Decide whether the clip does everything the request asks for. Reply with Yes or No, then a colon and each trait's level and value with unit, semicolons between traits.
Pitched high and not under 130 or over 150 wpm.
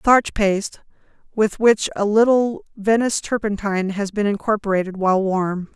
Yes: high, 205 Hz; slow, 135 wpm